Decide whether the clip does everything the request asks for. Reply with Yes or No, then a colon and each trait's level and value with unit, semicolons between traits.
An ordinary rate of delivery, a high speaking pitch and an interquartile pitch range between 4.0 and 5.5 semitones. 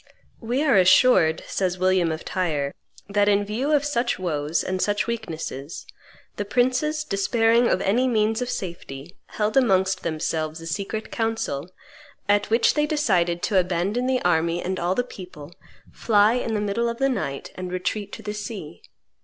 Yes: average, 170 wpm; high, 200 Hz; average, 5.0 semitones